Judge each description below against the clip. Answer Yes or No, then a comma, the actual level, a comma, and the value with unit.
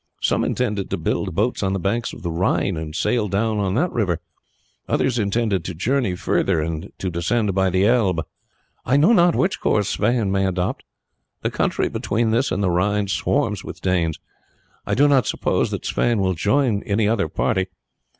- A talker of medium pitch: No, low, 100 Hz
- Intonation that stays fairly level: No, average, 4.2 semitones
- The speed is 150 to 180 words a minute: No, average, 190 wpm